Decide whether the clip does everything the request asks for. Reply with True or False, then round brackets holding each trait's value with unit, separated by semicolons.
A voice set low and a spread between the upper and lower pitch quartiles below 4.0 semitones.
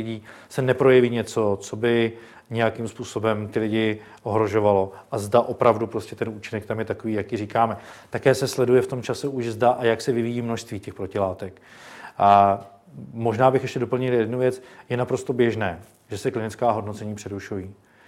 True (115 Hz; 2.6 semitones)